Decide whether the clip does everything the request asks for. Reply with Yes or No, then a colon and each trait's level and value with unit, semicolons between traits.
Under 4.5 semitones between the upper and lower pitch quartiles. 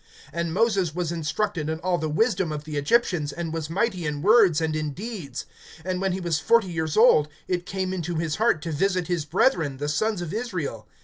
Yes: average, 3.7 semitones